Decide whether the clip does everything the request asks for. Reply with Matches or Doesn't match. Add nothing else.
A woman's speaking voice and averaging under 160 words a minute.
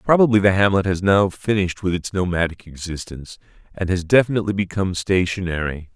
Doesn't match